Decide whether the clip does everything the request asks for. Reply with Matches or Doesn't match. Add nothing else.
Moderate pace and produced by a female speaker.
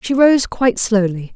Matches